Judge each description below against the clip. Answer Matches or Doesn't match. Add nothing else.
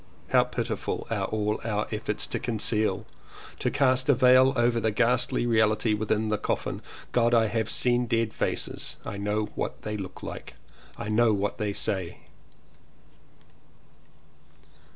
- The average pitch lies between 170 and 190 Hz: Doesn't match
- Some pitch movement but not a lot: Doesn't match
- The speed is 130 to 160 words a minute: Matches